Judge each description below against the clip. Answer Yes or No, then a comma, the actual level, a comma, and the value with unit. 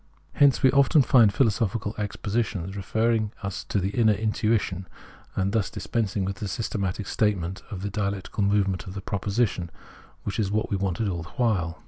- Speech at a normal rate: Yes, average, 170 wpm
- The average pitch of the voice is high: No, low, 100 Hz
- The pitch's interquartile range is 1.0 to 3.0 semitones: Yes, narrow, 2.5 semitones